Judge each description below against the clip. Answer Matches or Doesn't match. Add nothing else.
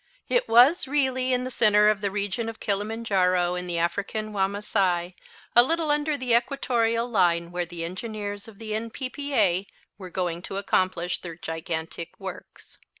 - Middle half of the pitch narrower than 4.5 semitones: Doesn't match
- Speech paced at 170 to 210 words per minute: Doesn't match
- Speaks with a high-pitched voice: Matches